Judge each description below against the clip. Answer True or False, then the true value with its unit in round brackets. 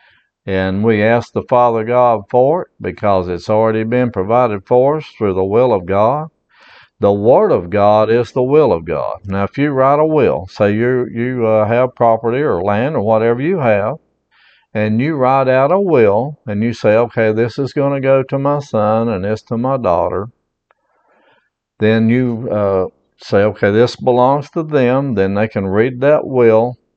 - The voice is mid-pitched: False (115 Hz)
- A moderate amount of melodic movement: True (3.3 semitones)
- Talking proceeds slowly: False (185 wpm)